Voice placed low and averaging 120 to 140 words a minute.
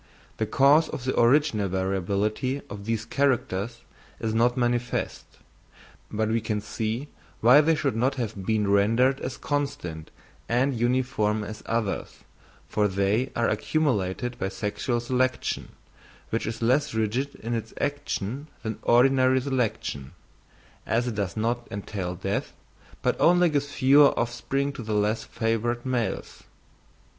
Yes: low, 115 Hz; slow, 135 wpm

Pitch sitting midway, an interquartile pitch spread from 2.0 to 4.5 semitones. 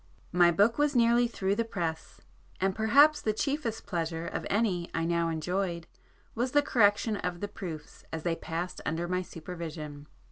No: medium, 180 Hz; average, 5.1 semitones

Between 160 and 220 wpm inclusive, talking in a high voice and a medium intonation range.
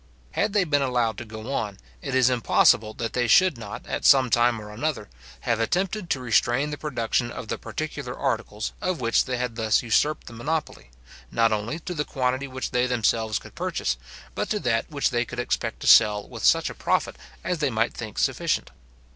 No: fast, 205 wpm; low, 120 Hz; average, 4.1 semitones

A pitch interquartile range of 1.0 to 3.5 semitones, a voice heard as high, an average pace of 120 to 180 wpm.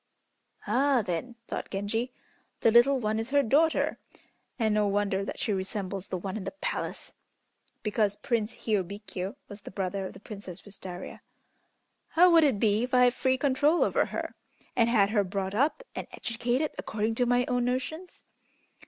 No: average, 4.0 semitones; high, 220 Hz; average, 175 wpm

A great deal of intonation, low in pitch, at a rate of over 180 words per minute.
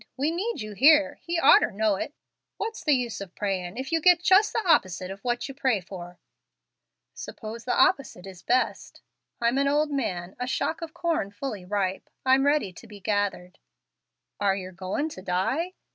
No: wide, 7.5 semitones; high, 235 Hz; average, 190 wpm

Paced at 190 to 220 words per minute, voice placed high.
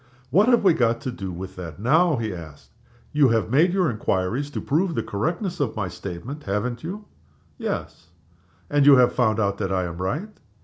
No: average, 195 wpm; low, 120 Hz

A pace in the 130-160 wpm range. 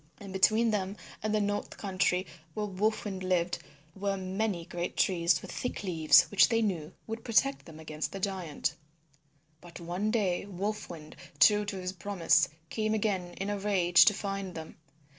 No: average, 175 wpm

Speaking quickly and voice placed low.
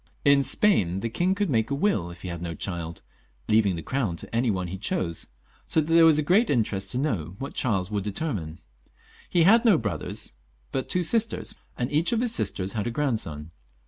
Yes: fast, 210 wpm; low, 115 Hz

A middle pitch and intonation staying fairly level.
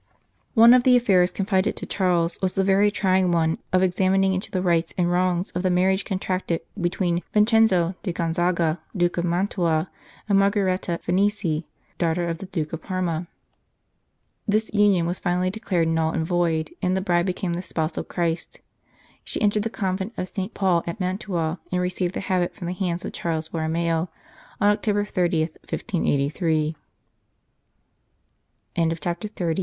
Yes: medium, 180 Hz; narrow, 2.3 semitones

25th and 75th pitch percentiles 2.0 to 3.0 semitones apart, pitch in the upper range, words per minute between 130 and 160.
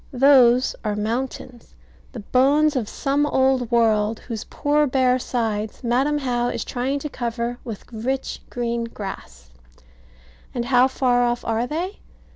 Yes: narrow, 2.5 semitones; high, 245 Hz; average, 140 wpm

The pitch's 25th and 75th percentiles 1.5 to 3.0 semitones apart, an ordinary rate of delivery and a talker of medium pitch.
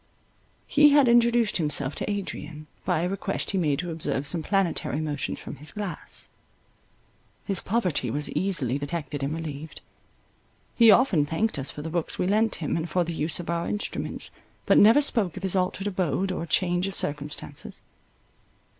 No: average, 4.8 semitones; average, 170 wpm; medium, 175 Hz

